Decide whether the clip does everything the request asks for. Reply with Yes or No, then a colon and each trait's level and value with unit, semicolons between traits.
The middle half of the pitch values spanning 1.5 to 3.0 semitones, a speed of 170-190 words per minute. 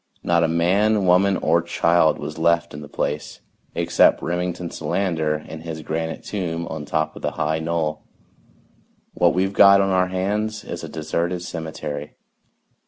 No: average, 2.7 semitones; average, 160 wpm